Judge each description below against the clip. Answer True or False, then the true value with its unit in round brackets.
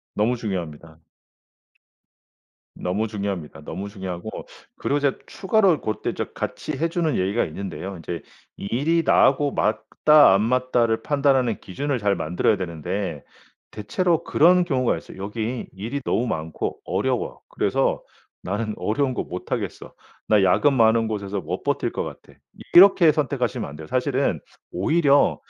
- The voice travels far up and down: True (6.7 semitones)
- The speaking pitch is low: True (110 Hz)